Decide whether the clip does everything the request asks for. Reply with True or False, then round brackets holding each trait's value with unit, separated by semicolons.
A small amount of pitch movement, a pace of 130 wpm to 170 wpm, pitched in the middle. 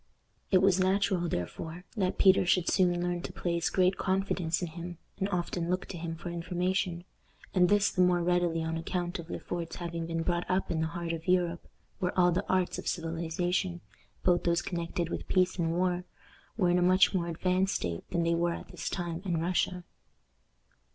False (1.4 semitones; 200 wpm; 175 Hz)